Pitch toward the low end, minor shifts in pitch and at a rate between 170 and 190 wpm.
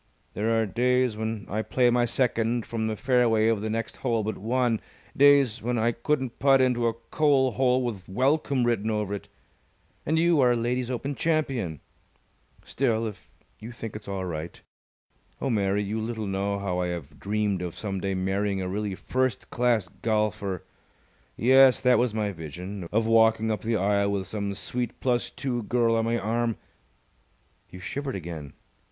No: low, 115 Hz; average, 3.5 semitones; average, 175 wpm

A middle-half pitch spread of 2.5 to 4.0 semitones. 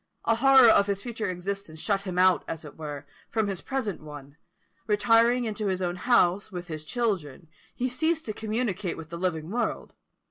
No: average, 5.1 semitones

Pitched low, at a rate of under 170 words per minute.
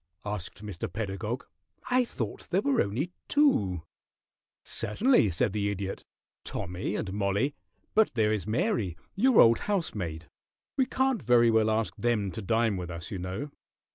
Yes: low, 110 Hz; average, 155 wpm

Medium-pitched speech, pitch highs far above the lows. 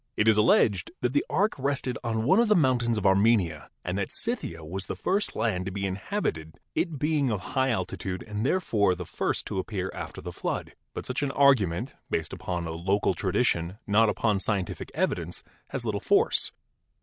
No: low, 105 Hz; wide, 6.0 semitones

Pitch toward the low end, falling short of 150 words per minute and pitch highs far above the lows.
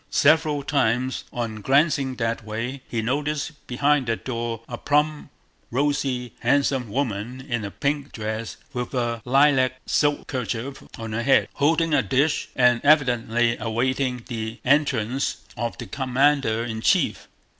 No: low, 130 Hz; average, 140 wpm; average, 3.4 semitones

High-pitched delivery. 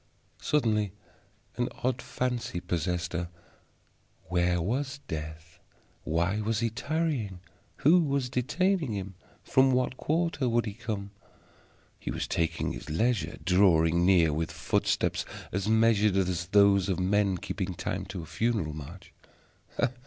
No: low, 100 Hz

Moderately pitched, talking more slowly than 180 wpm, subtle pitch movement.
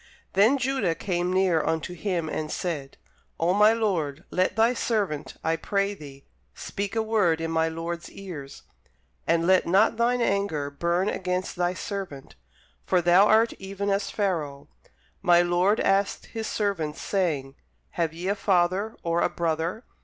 No: medium, 180 Hz; average, 155 wpm; average, 3.7 semitones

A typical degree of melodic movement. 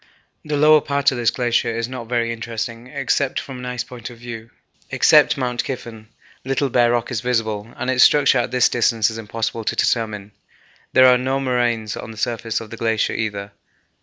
No: narrow, 2.0 semitones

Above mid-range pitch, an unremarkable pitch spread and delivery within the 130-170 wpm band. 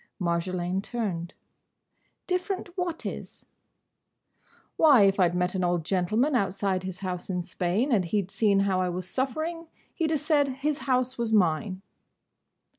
No: high, 200 Hz; wide, 6.9 semitones; average, 160 wpm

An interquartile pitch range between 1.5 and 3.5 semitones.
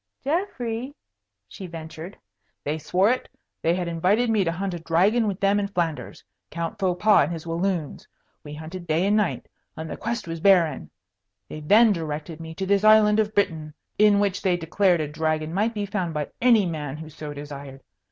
No: average, 4.6 semitones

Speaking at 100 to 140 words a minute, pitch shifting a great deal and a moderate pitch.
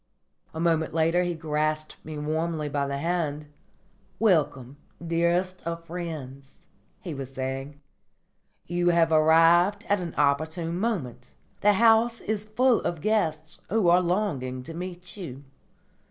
No: slow, 135 wpm; average, 3.2 semitones; medium, 165 Hz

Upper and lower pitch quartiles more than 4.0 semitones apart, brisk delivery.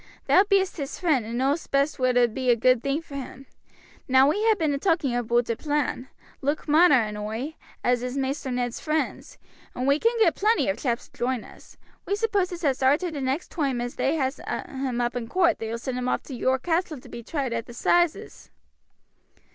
Yes: average, 4.5 semitones; fast, 220 wpm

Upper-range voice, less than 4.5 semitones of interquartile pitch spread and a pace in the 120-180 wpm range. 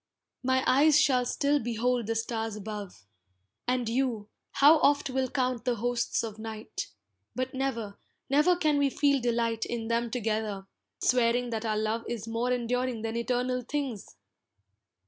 Yes: high, 240 Hz; narrow, 2.6 semitones; average, 150 wpm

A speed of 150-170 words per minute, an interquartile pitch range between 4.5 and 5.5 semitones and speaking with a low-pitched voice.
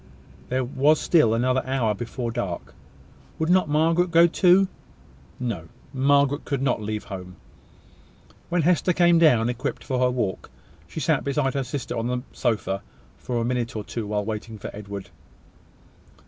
Yes: average, 160 wpm; average, 4.9 semitones; low, 125 Hz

